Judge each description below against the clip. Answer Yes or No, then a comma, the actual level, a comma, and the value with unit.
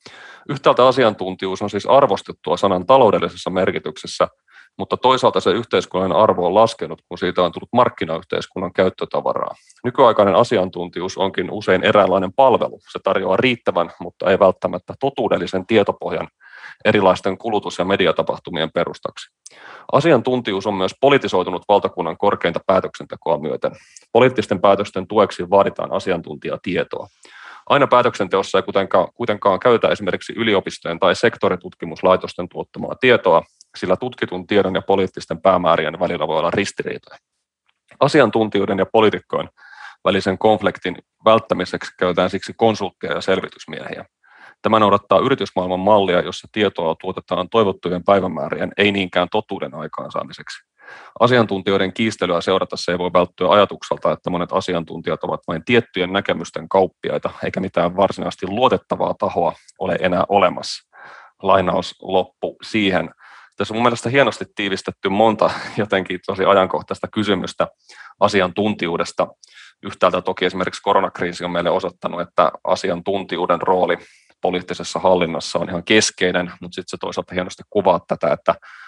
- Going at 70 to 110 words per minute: No, average, 120 wpm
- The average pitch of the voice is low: Yes, very low, 95 Hz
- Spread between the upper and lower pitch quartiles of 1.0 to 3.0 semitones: Yes, narrow, 2.5 semitones